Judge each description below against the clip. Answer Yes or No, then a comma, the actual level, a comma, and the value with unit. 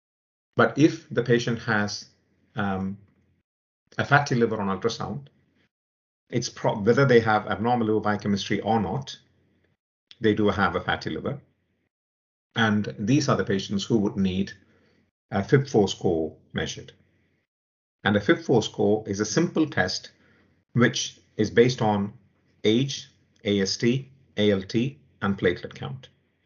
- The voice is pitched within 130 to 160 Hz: No, low, 105 Hz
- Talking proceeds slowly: Yes, slow, 130 wpm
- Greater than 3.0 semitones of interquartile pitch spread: Yes, average, 3.4 semitones